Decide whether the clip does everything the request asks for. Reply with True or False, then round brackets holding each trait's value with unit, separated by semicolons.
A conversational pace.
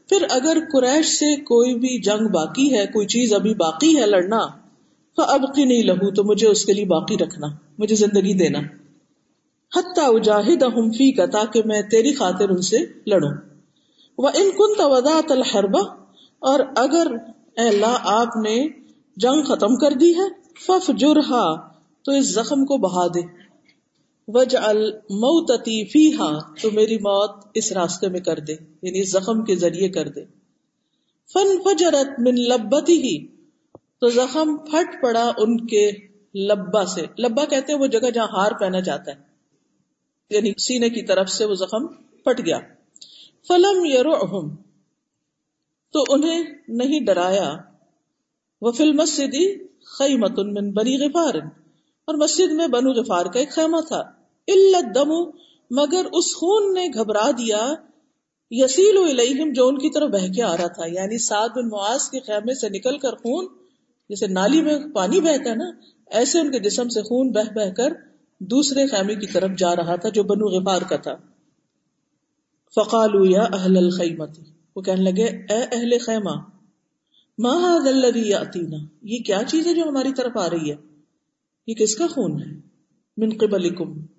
True (160 wpm)